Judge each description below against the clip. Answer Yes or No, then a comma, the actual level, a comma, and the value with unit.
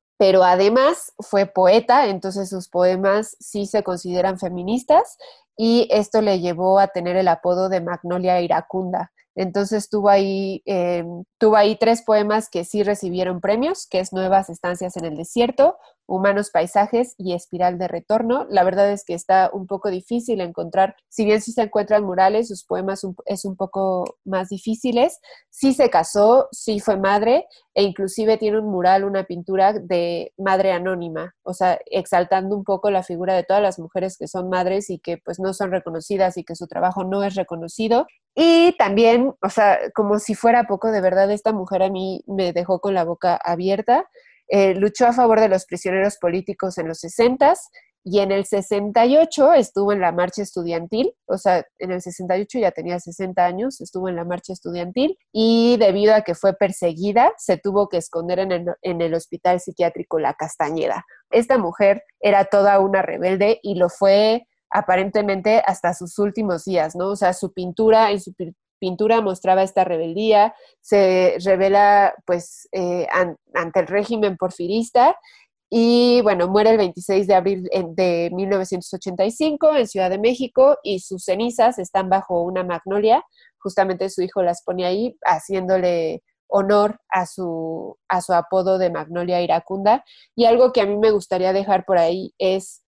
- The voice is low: No, high, 195 Hz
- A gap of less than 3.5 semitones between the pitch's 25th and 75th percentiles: Yes, average, 2.8 semitones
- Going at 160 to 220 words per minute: Yes, average, 170 wpm